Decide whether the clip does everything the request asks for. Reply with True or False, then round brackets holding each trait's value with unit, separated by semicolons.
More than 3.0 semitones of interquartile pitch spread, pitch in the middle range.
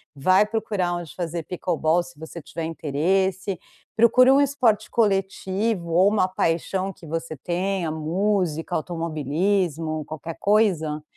True (3.5 semitones; 175 Hz)